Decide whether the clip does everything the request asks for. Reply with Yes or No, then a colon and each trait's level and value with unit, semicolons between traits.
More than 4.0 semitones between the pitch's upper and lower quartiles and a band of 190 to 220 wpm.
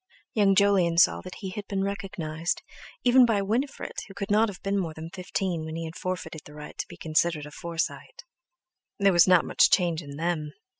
No: average, 3.5 semitones; fast, 205 wpm